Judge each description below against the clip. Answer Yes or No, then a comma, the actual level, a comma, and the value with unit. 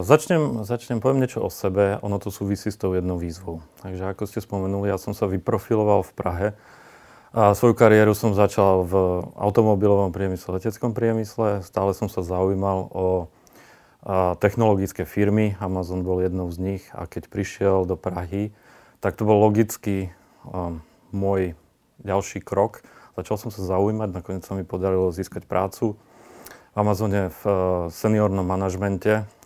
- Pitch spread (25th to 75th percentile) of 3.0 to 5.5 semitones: No, narrow, 2.4 semitones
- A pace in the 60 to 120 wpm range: No, average, 145 wpm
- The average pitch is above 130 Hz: No, low, 100 Hz